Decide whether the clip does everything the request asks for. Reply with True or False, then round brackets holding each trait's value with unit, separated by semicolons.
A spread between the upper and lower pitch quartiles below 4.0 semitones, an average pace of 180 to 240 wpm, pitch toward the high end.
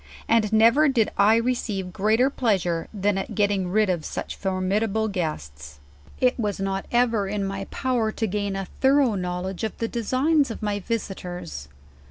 False (3.3 semitones; 170 wpm; 205 Hz)